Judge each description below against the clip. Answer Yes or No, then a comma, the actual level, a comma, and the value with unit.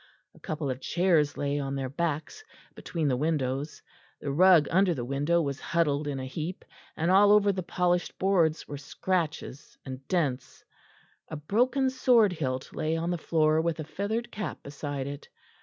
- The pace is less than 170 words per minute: No, average, 175 wpm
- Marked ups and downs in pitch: No, average, 4.2 semitones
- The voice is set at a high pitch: No, medium, 160 Hz